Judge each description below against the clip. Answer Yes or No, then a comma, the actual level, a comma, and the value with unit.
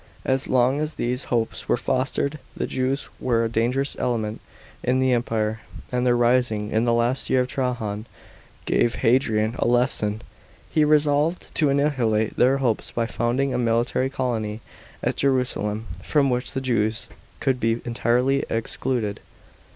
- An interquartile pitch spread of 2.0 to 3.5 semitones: Yes, narrow, 2.6 semitones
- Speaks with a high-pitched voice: No, low, 125 Hz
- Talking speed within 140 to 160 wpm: Yes, average, 155 wpm